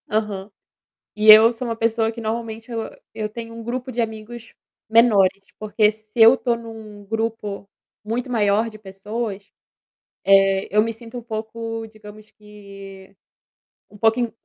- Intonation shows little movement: Yes, narrow, 1.6 semitones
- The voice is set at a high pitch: Yes, high, 220 Hz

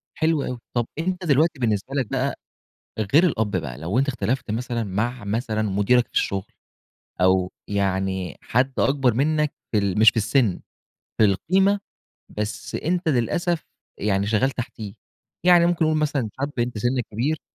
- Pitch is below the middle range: Yes, low, 120 Hz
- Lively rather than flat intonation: Yes, wide, 5.8 semitones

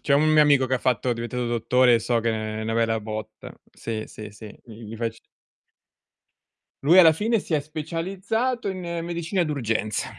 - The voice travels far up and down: Yes, wide, 6.5 semitones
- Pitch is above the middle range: No, low, 125 Hz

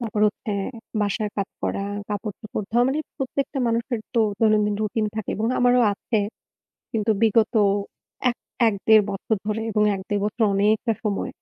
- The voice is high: Yes, high, 215 Hz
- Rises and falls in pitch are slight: Yes, narrow, 1.8 semitones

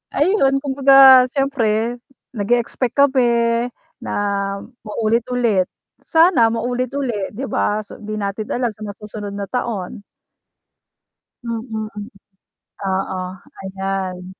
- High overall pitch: Yes, high, 230 Hz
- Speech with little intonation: No, average, 3.5 semitones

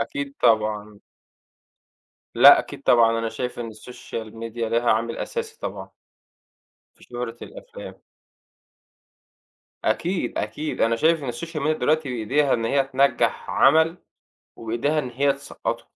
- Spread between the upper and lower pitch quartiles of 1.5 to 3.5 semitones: No, wide, 5.4 semitones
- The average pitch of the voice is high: No, low, 130 Hz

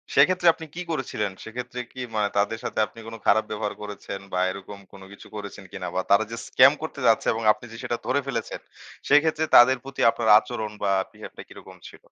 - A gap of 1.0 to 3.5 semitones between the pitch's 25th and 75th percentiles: No, average, 4.3 semitones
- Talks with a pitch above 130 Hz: No, low, 115 Hz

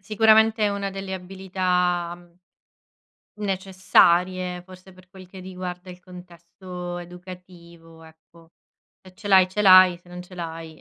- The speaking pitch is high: No, medium, 180 Hz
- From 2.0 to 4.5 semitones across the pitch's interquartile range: No, narrow, 1.3 semitones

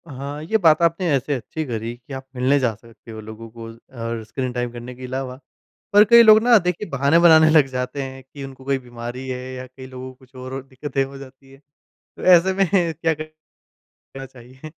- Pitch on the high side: No, low, 130 Hz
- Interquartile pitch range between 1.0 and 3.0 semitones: No, average, 3.8 semitones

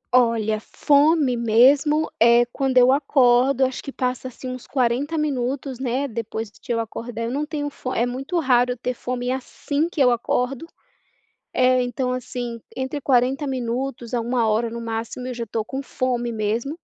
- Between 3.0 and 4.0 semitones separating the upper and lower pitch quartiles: No, narrow, 2.4 semitones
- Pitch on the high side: Yes, very high, 250 Hz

